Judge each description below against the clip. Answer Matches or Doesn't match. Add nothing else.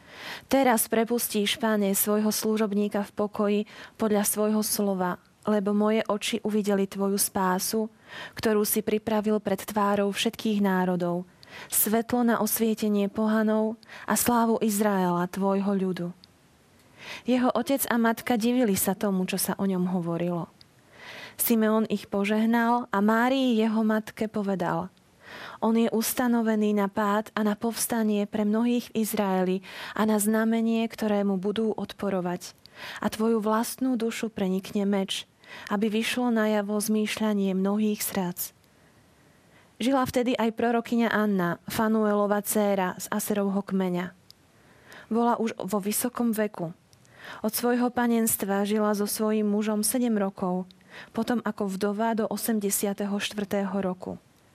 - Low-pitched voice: Doesn't match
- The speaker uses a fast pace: Doesn't match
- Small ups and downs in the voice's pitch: Matches